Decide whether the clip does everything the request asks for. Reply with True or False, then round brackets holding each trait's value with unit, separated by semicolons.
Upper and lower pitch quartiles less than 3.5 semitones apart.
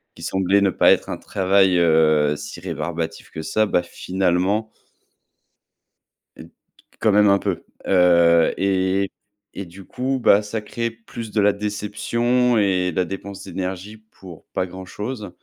True (2.9 semitones)